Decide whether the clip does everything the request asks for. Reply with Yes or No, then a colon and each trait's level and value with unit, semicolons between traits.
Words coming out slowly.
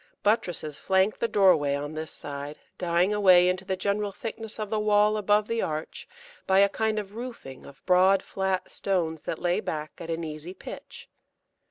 No: average, 180 wpm